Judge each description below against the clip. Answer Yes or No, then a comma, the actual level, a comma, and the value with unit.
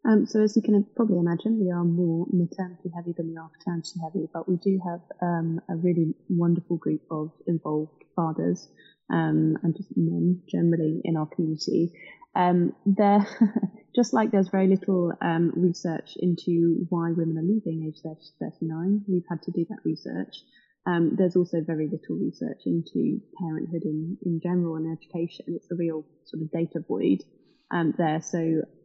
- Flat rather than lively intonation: Yes, narrow, 2.2 semitones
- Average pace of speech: Yes, average, 175 wpm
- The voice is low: No, medium, 170 Hz